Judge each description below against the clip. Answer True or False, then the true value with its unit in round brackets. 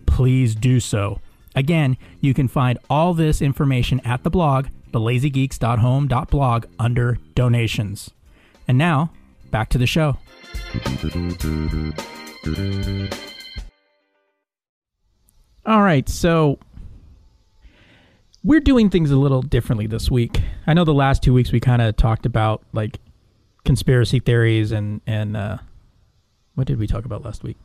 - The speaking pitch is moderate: False (120 Hz)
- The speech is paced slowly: True (125 wpm)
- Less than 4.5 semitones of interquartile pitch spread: False (5.1 semitones)